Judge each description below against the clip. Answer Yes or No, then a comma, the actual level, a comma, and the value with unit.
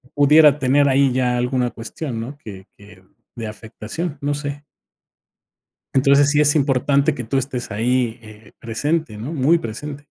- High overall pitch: No, low, 135 Hz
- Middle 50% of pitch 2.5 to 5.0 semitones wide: Yes, average, 4.0 semitones